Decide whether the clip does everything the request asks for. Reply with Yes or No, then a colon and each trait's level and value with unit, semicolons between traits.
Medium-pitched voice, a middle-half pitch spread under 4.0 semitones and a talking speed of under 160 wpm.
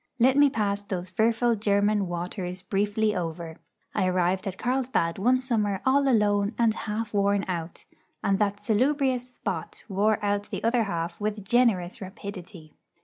No: high, 205 Hz; average, 3.6 semitones; average, 150 wpm